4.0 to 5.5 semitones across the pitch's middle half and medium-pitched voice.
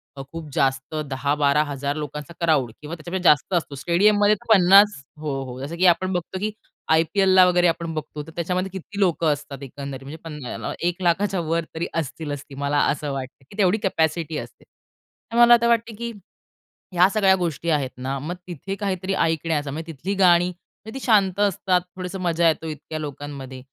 Yes: average, 4.3 semitones; medium, 165 Hz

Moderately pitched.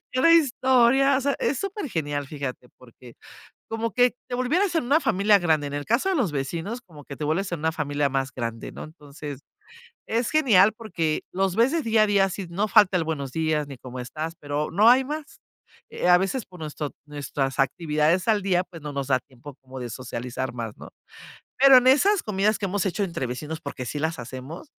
Yes: medium, 170 Hz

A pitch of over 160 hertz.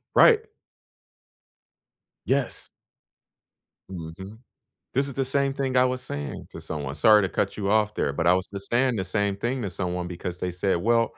No: low, 100 Hz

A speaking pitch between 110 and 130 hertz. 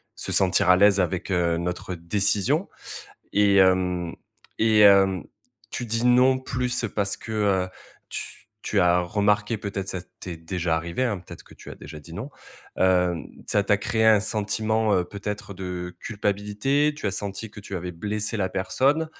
No: low, 100 Hz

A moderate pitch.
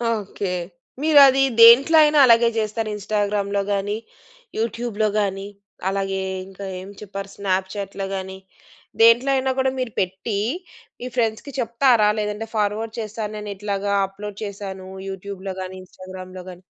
No: high, 205 Hz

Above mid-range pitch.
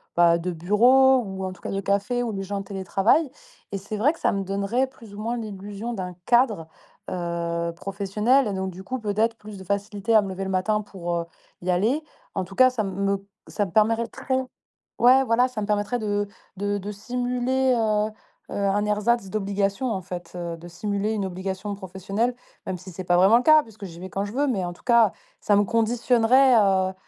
Yes: high, 205 Hz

